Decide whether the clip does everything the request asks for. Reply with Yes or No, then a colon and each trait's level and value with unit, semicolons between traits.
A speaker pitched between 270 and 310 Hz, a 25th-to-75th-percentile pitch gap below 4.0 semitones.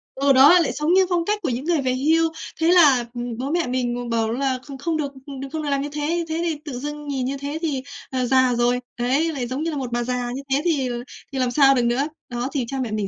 Yes: very high, 275 Hz; average, 3.5 semitones